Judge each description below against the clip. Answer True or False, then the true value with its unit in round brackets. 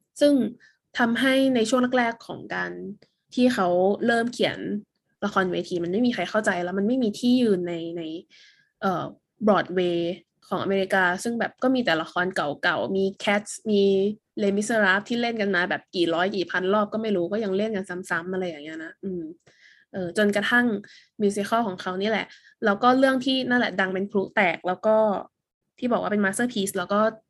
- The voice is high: True (205 Hz)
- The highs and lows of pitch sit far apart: False (4.0 semitones)